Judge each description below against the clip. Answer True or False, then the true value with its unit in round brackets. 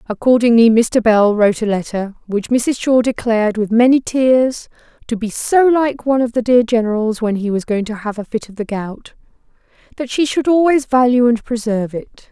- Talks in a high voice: True (230 Hz)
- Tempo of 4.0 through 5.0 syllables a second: False (5.2 syllables/s)